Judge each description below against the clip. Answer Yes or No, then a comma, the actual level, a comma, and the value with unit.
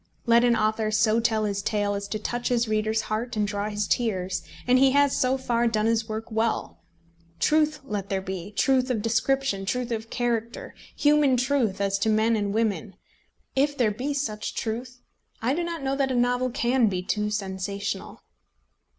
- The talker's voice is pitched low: No, high, 225 Hz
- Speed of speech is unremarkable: Yes, average, 185 wpm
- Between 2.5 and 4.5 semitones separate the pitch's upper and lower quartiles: Yes, average, 3.1 semitones